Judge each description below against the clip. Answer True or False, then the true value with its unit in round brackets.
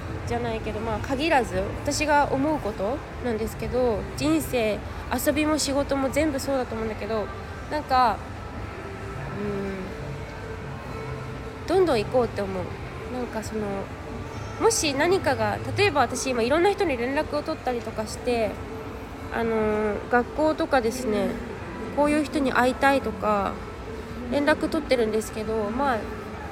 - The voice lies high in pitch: True (255 Hz)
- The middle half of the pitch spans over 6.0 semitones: False (5.6 semitones)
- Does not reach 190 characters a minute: False (290 characters per minute)